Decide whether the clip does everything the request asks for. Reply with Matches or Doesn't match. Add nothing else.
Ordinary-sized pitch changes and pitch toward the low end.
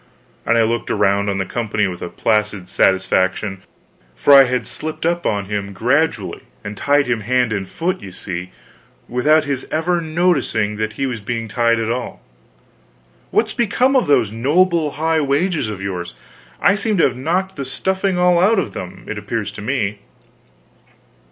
Doesn't match